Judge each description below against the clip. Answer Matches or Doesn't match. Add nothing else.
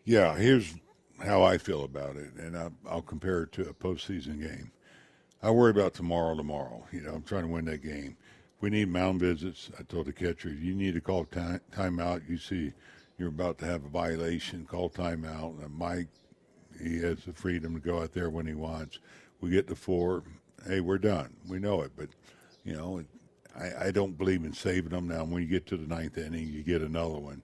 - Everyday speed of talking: Doesn't match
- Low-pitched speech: Matches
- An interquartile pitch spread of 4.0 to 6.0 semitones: Doesn't match